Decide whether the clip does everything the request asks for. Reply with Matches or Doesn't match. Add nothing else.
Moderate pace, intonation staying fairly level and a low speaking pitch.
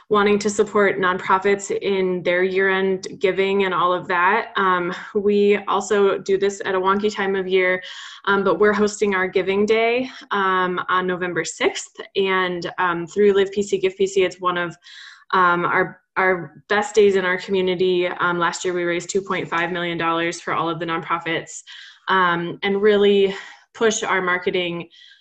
Doesn't match